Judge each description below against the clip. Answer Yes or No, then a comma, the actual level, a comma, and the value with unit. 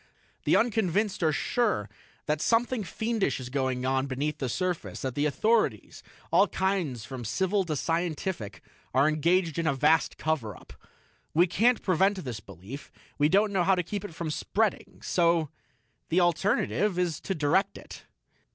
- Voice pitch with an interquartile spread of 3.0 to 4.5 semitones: No, wide, 5.5 semitones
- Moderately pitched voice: Yes, medium, 170 Hz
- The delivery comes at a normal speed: Yes, average, 160 wpm